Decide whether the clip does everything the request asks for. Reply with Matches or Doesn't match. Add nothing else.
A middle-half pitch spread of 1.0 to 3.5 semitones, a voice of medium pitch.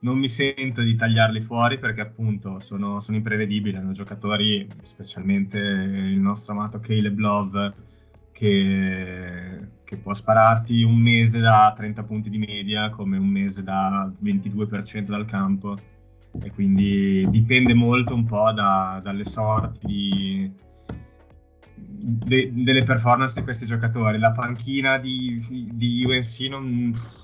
Doesn't match